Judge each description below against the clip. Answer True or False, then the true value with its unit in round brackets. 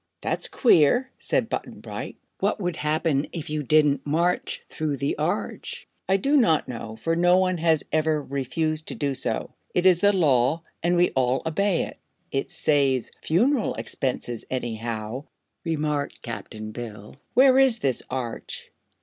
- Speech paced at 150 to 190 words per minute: True (155 wpm)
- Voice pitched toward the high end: False (155 Hz)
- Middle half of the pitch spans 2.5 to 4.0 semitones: False (5.2 semitones)